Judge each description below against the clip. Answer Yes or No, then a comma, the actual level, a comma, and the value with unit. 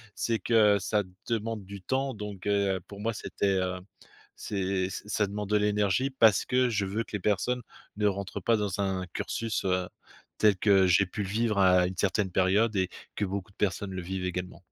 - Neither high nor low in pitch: No, low, 100 Hz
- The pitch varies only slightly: Yes, narrow, 2.2 semitones